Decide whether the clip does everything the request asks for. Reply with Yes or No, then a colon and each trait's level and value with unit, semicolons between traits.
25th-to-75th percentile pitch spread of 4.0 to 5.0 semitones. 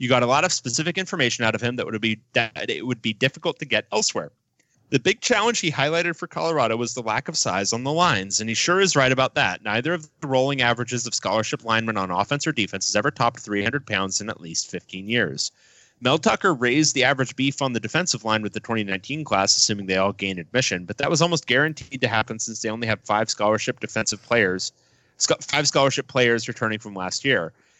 Yes: average, 4.6 semitones